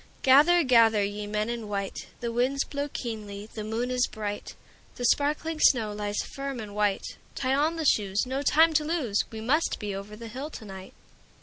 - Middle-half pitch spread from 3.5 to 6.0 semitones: Yes, average, 4.9 semitones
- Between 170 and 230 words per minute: Yes, average, 175 wpm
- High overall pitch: Yes, high, 235 Hz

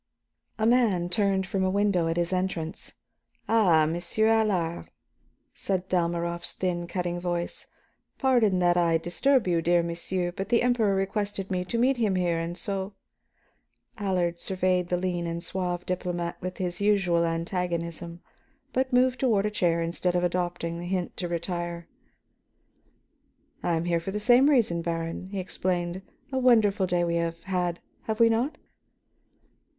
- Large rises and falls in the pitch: No, average, 2.8 semitones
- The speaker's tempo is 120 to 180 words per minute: Yes, average, 155 wpm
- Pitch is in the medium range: Yes, medium, 180 Hz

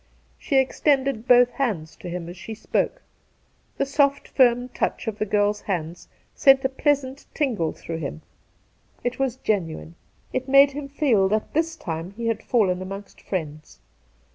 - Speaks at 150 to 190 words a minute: Yes, average, 160 wpm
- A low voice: No, high, 230 Hz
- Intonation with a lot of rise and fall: Yes, wide, 6.4 semitones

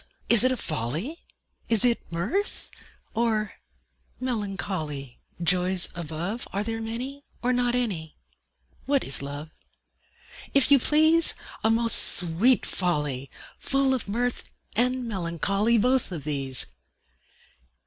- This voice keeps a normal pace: No, slow, 120 wpm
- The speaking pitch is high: Yes, high, 215 Hz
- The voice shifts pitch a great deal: Yes, wide, 6.8 semitones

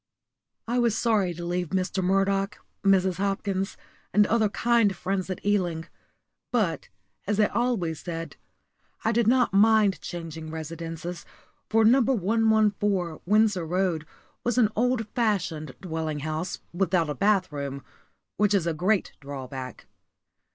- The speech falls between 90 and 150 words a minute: Yes, slow, 135 wpm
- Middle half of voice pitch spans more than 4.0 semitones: Yes, average, 4.4 semitones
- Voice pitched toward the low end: No, high, 195 Hz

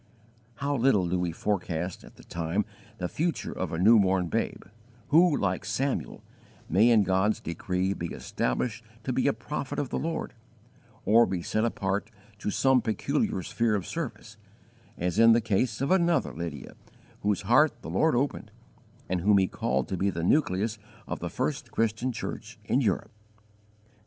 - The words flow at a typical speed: Yes, average, 170 wpm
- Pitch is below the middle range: Yes, low, 105 Hz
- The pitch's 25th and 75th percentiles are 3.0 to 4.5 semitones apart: No, wide, 5.4 semitones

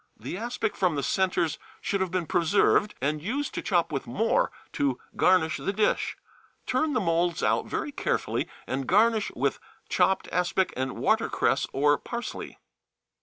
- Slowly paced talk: No, average, 155 wpm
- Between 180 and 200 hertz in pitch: Yes, medium, 185 Hz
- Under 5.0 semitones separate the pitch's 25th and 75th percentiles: No, wide, 5.4 semitones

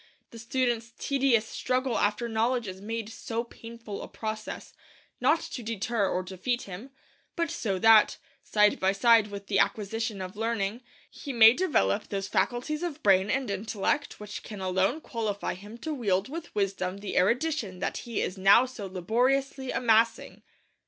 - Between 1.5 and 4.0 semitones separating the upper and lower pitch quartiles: Yes, average, 3.6 semitones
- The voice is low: No, high, 225 Hz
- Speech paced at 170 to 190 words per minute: No, average, 160 wpm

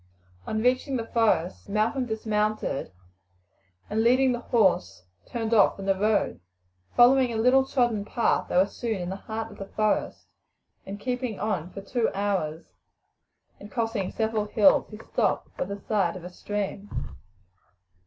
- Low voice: No, high, 215 Hz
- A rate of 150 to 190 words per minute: Yes, average, 160 wpm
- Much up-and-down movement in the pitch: No, average, 2.9 semitones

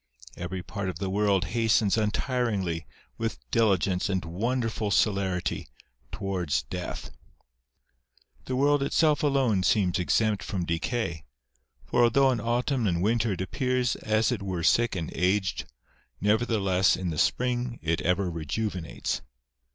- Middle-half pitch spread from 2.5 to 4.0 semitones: No, average, 4.6 semitones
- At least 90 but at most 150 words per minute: Yes, slow, 135 wpm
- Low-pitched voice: Yes, low, 100 Hz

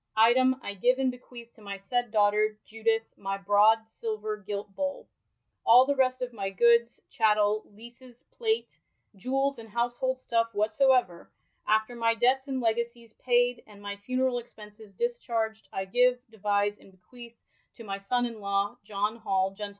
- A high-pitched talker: Yes, high, 225 Hz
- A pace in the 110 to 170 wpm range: Yes, average, 160 wpm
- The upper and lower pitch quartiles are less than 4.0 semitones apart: Yes, average, 3.1 semitones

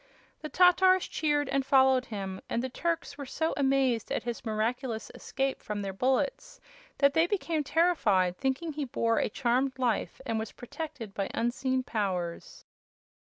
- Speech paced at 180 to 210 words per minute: No, average, 155 wpm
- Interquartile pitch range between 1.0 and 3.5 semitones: No, average, 4.5 semitones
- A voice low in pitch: No, very high, 260 Hz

